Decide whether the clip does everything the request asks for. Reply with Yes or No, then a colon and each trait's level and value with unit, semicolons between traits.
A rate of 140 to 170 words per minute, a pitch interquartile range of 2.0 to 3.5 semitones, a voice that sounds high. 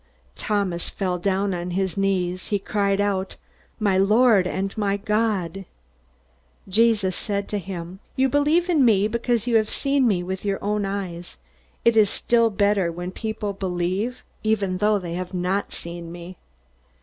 Yes: average, 160 wpm; average, 2.8 semitones; high, 200 Hz